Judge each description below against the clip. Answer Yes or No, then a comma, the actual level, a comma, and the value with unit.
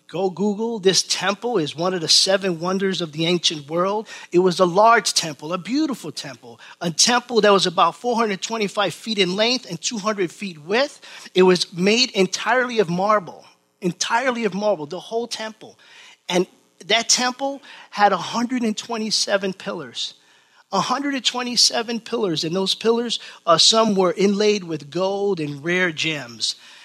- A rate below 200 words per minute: Yes, average, 150 wpm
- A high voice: Yes, high, 200 Hz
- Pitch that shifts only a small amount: No, average, 4.3 semitones